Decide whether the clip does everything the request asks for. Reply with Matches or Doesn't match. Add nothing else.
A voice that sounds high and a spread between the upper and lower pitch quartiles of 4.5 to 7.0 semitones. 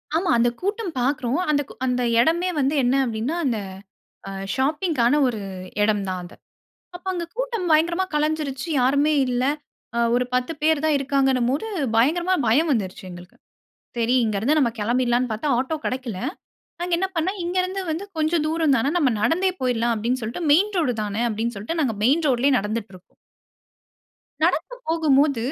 Matches